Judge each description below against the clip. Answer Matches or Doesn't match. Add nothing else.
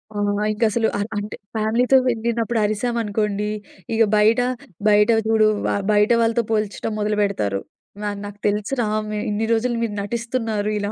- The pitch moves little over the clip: Matches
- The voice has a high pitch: Matches